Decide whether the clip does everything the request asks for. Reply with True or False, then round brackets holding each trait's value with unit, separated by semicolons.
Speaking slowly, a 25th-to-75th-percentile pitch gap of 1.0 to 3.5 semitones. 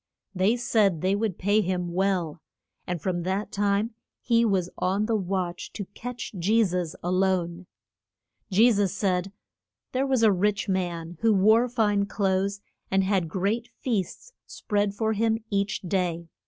False (155 wpm; 3.0 semitones)